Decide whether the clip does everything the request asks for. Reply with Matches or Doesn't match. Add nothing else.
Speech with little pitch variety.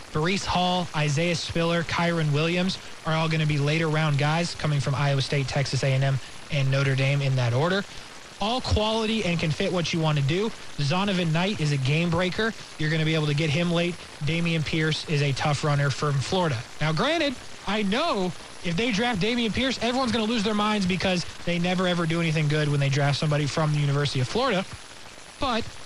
Doesn't match